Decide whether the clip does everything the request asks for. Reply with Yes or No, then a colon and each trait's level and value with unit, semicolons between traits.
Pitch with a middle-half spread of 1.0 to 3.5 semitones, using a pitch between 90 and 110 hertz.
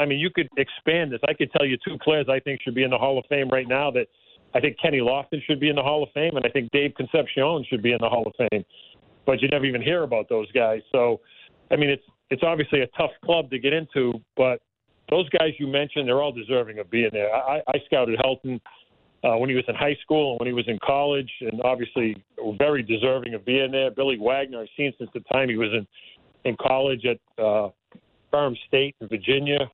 No: average, 3.2 semitones; low, 135 Hz